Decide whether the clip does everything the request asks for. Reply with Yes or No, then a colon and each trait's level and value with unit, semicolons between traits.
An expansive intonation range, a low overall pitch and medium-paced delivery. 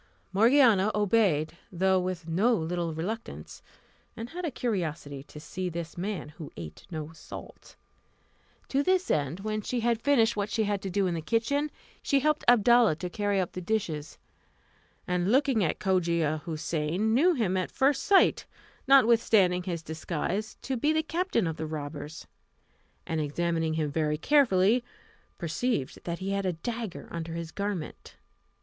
No: wide, 6.0 semitones; high, 190 Hz; average, 160 wpm